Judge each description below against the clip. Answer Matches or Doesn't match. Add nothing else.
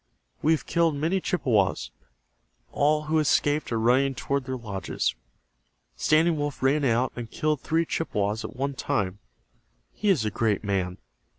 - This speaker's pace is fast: Doesn't match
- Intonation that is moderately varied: Doesn't match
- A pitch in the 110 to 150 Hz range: Matches